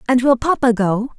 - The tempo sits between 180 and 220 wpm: Yes, average, 200 wpm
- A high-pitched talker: Yes, high, 240 Hz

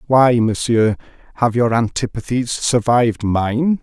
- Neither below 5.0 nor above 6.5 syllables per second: No, 4.1 syllables/s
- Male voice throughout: Yes, male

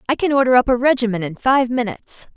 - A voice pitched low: No, high, 245 Hz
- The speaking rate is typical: No, fast, 230 wpm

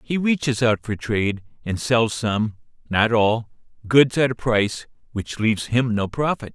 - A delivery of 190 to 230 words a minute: No, average, 175 wpm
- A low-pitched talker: Yes, low, 115 Hz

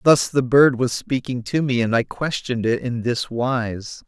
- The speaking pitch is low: Yes, low, 125 Hz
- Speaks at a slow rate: No, fast, 205 wpm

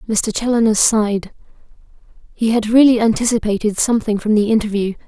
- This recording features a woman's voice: Yes, female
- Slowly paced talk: Yes, slow, 130 wpm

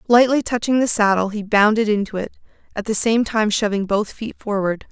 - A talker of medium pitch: No, high, 215 Hz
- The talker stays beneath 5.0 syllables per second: No, 5.4 syllables/s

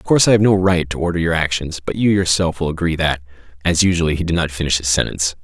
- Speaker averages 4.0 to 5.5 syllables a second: No, 6.7 syllables/s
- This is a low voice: Yes, very low, 85 Hz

